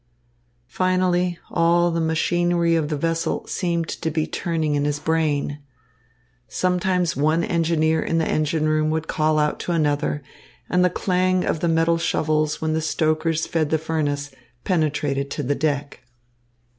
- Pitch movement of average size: No, narrow, 1.8 semitones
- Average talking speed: Yes, average, 155 wpm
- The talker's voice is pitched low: No, medium, 160 Hz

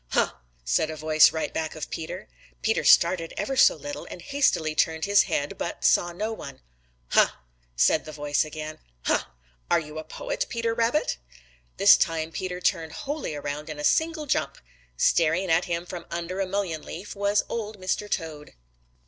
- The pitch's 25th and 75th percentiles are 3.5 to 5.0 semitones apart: Yes, average, 4.6 semitones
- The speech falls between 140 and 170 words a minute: No, average, 180 wpm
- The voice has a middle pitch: Yes, medium, 170 Hz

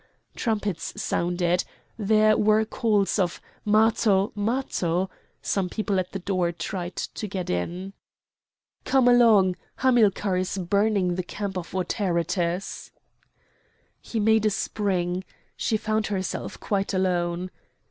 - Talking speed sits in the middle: No, slow, 115 wpm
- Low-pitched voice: No, high, 195 Hz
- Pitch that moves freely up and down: No, average, 3.0 semitones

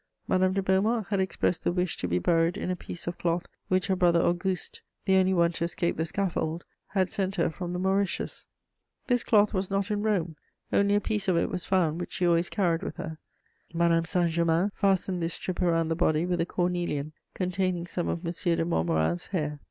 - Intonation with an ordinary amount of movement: No, narrow, 2.2 semitones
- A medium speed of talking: No, fast, 215 wpm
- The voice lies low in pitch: No, medium, 175 Hz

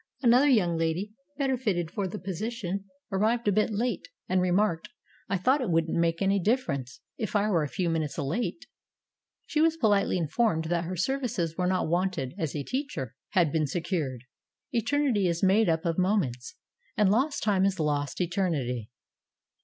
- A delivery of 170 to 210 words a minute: Yes, average, 175 wpm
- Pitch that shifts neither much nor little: Yes, average, 4.9 semitones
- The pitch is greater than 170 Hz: Yes, medium, 185 Hz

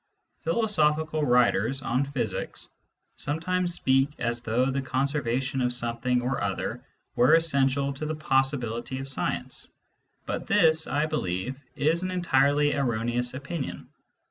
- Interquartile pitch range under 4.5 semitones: Yes, average, 3.7 semitones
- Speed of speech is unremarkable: No, slow, 125 wpm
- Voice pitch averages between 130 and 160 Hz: Yes, low, 135 Hz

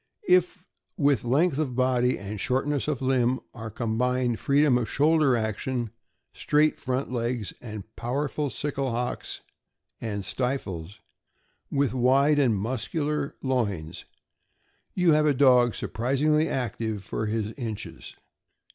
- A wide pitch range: No, average, 4.0 semitones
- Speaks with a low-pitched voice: Yes, low, 125 Hz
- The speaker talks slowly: Yes, slow, 125 wpm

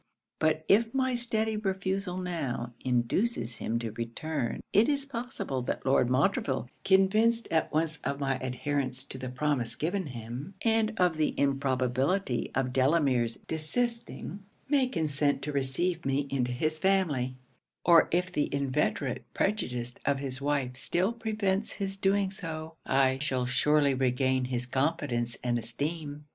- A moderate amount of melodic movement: No, wide, 6.7 semitones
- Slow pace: No, average, 145 wpm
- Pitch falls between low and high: Yes, medium, 145 Hz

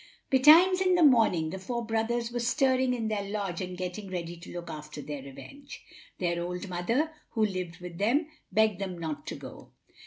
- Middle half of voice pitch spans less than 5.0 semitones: No, wide, 5.6 semitones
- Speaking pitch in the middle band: No, high, 200 Hz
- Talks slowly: No, average, 190 wpm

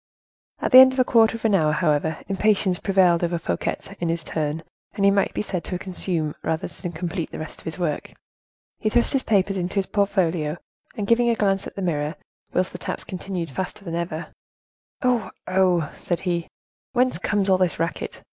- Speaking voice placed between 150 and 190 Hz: Yes, medium, 185 Hz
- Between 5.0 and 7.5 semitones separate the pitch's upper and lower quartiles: No, average, 3.3 semitones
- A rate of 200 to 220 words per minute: Yes, fast, 205 wpm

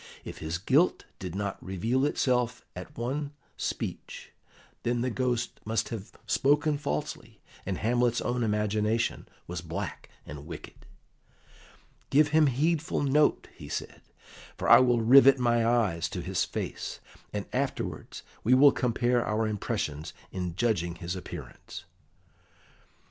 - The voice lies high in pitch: No, low, 115 Hz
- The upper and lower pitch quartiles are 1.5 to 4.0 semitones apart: No, average, 5.2 semitones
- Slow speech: Yes, slow, 130 wpm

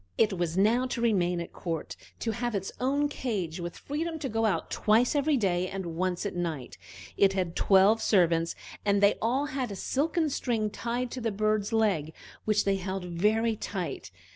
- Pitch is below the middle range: No, high, 210 Hz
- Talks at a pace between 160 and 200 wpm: Yes, average, 190 wpm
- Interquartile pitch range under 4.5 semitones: No, average, 4.8 semitones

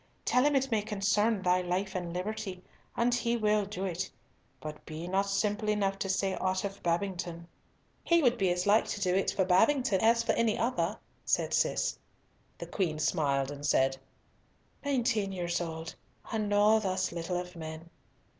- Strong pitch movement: No, average, 3.4 semitones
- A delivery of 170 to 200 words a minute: Yes, average, 175 wpm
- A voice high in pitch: Yes, high, 195 Hz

